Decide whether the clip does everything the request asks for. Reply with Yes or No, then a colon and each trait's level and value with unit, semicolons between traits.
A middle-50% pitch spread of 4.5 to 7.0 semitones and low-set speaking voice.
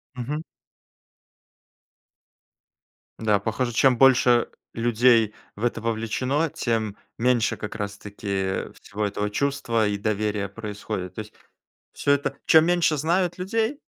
Yes: average, 4.9 semitones; low, 115 Hz